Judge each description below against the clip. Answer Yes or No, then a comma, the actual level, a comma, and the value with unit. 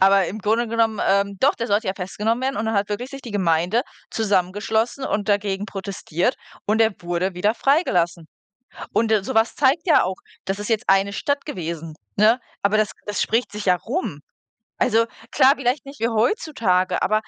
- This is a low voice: No, high, 210 Hz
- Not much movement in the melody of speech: No, average, 3.3 semitones